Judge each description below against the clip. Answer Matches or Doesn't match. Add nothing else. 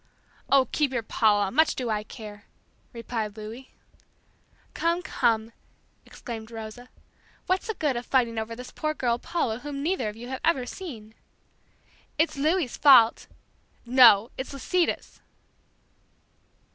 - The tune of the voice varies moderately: Matches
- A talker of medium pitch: Doesn't match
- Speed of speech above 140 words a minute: Doesn't match